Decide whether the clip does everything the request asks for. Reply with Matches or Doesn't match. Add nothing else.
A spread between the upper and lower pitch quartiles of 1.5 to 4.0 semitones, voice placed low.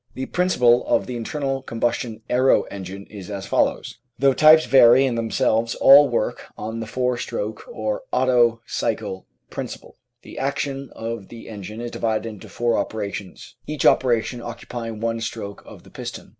Matches